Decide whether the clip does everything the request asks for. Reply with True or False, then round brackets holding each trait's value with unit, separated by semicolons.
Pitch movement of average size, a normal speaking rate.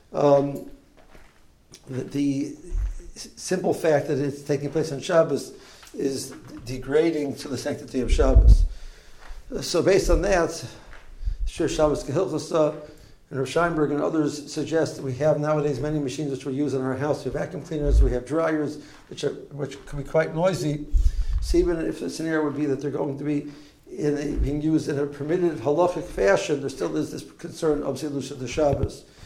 False (1.8 semitones; 175 wpm)